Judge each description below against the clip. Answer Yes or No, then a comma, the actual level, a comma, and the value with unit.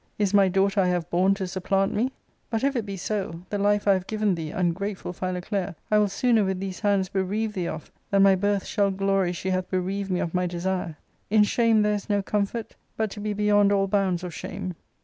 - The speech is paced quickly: Yes, fast, 230 wpm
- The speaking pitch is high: Yes, high, 195 Hz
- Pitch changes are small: Yes, narrow, 2.0 semitones